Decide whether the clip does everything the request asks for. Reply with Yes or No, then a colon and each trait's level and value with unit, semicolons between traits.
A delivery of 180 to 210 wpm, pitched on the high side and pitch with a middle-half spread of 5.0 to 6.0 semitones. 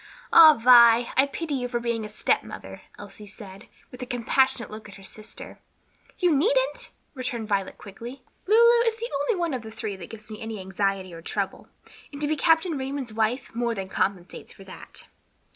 Yes: average, 190 wpm; high, 235 Hz; average, 5.3 semitones